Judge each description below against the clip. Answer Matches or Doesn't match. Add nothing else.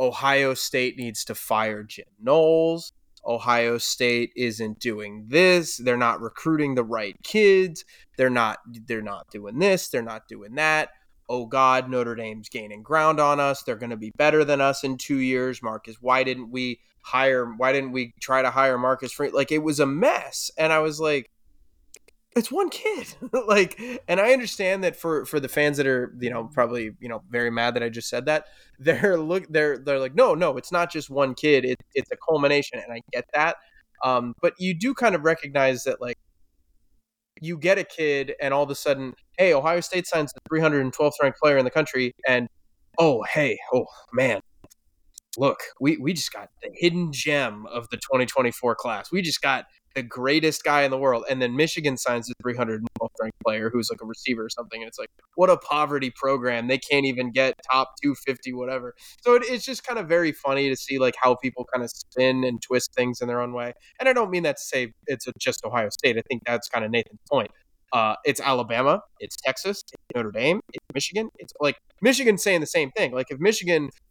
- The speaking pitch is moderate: Doesn't match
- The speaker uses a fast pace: Matches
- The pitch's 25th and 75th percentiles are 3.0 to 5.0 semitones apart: Matches